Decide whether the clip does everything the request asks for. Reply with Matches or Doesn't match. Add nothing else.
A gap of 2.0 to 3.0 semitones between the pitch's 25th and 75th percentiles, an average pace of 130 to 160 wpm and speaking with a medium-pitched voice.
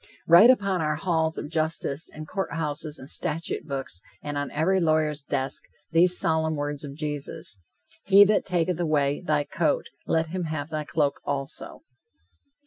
Matches